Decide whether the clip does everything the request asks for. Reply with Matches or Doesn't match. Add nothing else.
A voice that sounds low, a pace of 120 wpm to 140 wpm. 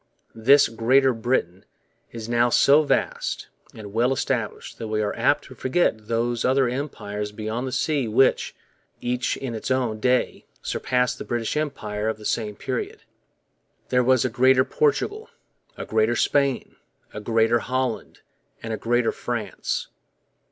Doesn't match